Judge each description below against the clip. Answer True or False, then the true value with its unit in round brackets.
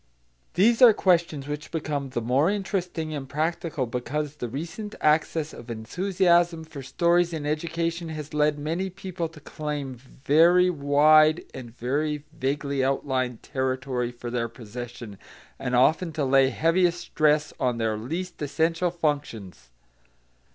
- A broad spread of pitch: False (4.2 semitones)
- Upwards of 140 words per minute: False (135 wpm)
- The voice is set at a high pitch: False (150 Hz)